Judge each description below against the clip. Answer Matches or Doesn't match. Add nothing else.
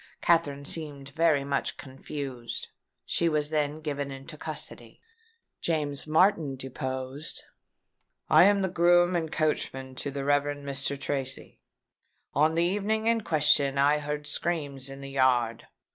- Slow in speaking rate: Matches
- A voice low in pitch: Doesn't match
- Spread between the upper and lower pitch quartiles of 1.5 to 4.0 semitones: Matches